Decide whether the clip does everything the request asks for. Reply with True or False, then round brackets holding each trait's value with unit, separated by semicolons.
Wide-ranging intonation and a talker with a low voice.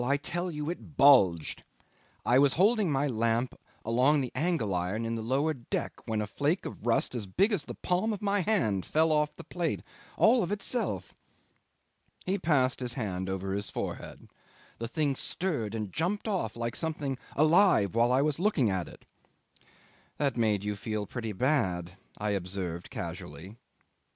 True (7.3 semitones; 130 Hz)